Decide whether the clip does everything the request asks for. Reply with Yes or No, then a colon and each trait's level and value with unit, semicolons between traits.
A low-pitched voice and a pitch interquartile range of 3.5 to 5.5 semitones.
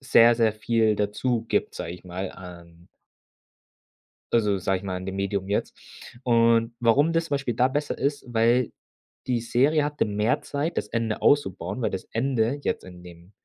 Yes: low, 115 Hz; average, 4.7 semitones